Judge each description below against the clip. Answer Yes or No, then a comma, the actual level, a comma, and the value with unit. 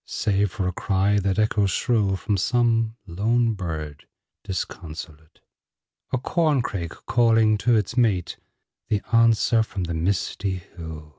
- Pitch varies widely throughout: No, average, 4.2 semitones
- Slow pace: Yes, slow, 130 wpm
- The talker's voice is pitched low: Yes, low, 100 Hz